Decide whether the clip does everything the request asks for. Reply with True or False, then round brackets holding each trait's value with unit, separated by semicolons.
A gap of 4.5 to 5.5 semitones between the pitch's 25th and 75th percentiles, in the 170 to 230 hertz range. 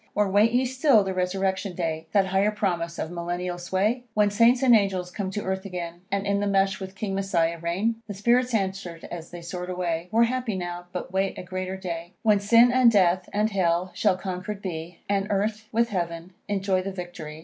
False (2.9 semitones; 190 Hz)